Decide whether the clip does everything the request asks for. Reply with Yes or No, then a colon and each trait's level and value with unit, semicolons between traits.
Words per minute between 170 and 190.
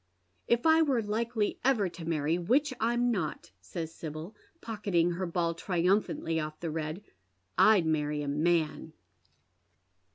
No: average, 150 wpm